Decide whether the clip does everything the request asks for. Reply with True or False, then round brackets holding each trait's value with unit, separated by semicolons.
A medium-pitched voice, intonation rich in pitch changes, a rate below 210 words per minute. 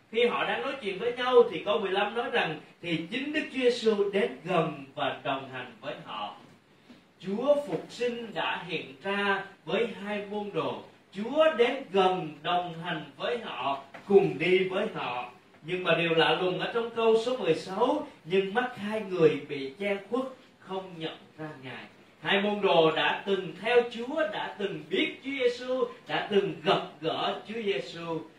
False (195 Hz; 6.5 semitones; 180 wpm)